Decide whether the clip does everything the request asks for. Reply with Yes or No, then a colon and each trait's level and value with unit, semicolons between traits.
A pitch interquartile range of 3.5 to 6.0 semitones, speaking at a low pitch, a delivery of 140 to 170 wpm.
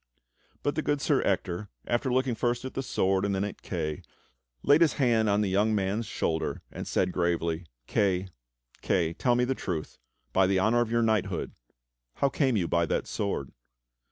No: average, 4.8 semitones; low, 105 Hz; average, 185 wpm